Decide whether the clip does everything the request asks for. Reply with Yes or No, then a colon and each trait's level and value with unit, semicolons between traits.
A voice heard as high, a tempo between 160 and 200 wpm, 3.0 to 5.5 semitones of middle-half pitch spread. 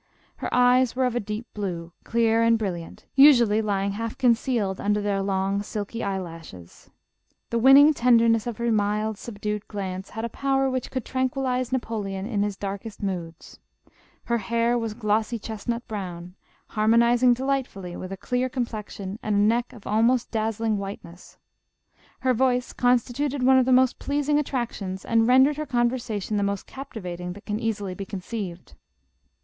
Yes: high, 225 Hz; average, 165 wpm; average, 3.7 semitones